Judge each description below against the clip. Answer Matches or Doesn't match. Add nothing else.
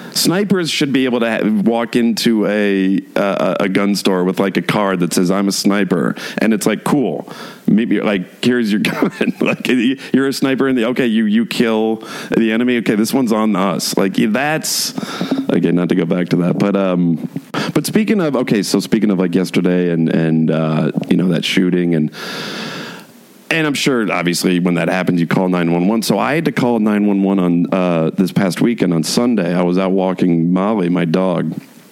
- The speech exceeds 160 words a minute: Matches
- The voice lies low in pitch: Matches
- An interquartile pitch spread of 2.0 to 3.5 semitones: Doesn't match